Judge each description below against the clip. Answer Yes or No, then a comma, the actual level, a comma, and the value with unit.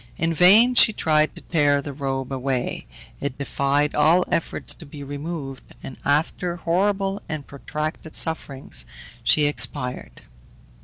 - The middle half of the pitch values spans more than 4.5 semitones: No, average, 3.2 semitones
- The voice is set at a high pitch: No, medium, 150 Hz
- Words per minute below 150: Yes, slow, 135 wpm